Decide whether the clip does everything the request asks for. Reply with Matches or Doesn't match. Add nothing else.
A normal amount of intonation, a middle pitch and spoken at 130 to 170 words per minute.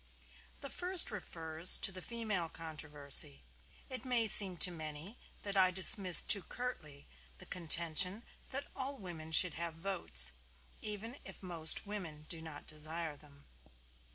Matches